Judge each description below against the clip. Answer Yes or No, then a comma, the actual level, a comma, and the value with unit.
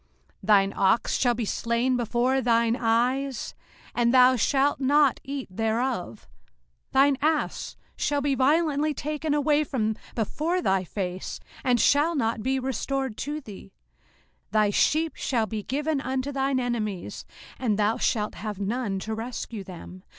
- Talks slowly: No, average, 145 wpm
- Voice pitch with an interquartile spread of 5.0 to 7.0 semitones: No, average, 4.2 semitones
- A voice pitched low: No, very high, 250 Hz